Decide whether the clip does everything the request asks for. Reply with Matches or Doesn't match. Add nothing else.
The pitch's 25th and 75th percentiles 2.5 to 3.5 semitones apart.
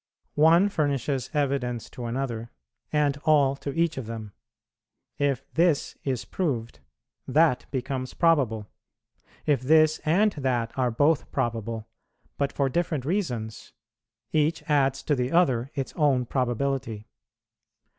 Doesn't match